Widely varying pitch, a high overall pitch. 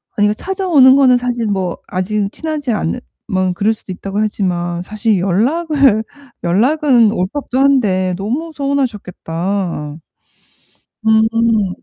Yes: wide, 5.9 semitones; high, 215 Hz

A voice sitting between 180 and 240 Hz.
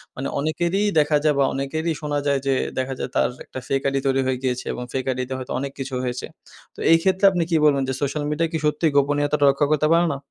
No: medium, 140 Hz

